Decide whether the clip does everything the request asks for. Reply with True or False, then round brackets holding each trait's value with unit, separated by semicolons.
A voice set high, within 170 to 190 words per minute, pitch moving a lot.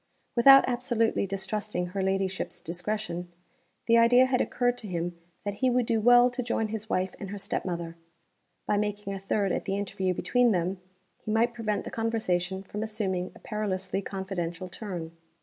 False (205 Hz; 175 wpm; 3.4 semitones)